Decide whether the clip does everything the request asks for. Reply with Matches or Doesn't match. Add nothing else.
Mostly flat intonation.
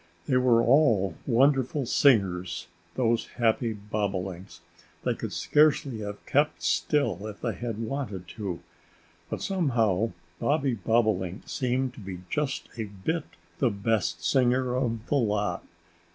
Doesn't match